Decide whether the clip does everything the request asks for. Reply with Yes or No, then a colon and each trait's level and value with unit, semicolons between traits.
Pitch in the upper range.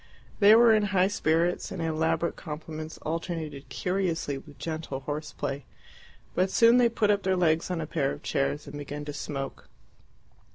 No: medium, 160 Hz